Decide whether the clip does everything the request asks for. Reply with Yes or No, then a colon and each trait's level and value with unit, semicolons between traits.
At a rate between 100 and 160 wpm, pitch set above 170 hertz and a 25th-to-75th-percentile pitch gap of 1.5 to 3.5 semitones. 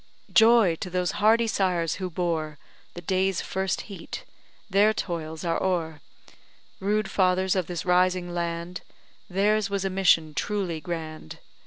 Yes: average, 140 wpm; medium, 185 Hz; narrow, 2.6 semitones